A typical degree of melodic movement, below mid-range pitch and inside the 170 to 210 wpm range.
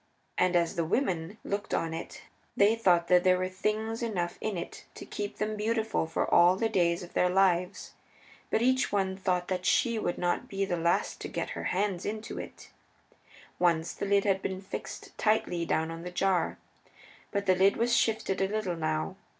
No: average, 3.1 semitones; high, 190 Hz; average, 195 wpm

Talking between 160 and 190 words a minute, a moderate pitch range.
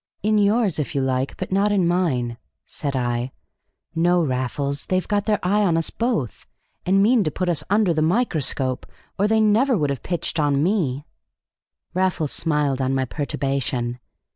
No: average, 170 wpm; wide, 6.7 semitones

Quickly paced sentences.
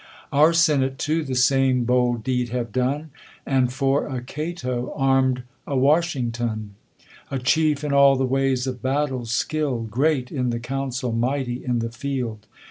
No: average, 155 wpm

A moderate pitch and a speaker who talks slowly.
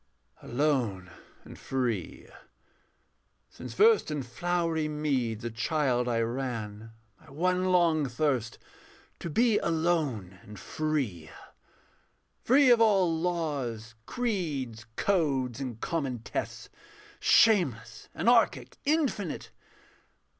Yes: medium, 145 Hz; slow, 95 wpm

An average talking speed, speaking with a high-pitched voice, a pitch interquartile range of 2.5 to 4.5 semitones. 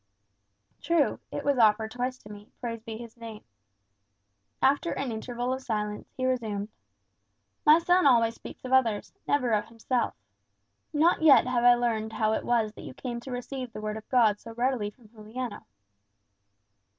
Yes: average, 170 wpm; high, 235 Hz; average, 2.8 semitones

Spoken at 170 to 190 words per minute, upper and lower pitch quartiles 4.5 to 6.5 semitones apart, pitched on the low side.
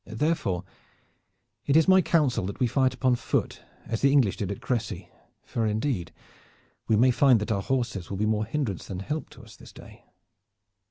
Yes: average, 185 wpm; wide, 5.4 semitones; low, 115 Hz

